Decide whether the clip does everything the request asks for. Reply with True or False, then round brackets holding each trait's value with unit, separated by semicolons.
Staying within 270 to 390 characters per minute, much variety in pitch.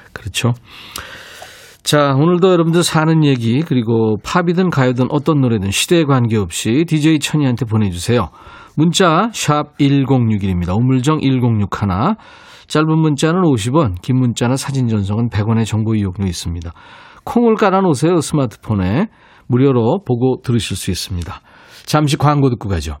True (305 characters per minute; 6.2 semitones)